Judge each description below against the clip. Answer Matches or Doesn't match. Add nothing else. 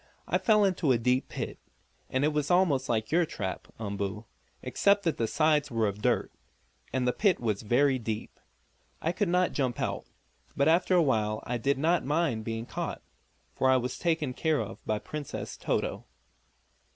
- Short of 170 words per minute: Doesn't match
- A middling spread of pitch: Doesn't match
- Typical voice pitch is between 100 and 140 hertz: Matches